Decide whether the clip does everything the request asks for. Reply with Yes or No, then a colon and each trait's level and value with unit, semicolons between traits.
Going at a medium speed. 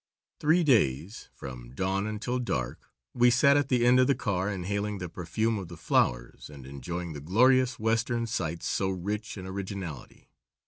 Yes: average, 170 wpm